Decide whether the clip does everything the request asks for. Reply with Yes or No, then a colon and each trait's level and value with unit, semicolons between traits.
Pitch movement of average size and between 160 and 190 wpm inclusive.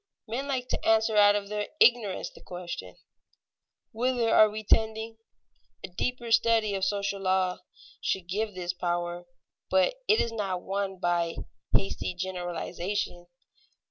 No: average, 3.5 semitones; average, 140 wpm